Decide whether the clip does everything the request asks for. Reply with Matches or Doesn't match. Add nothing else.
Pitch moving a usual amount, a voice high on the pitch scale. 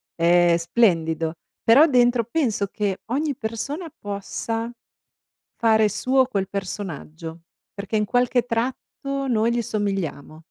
Matches